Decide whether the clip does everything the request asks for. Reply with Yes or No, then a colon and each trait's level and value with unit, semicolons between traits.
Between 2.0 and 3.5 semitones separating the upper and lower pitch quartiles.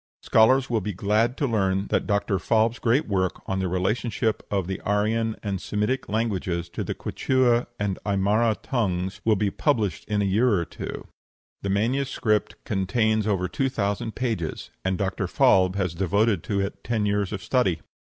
Yes: average, 3.0 semitones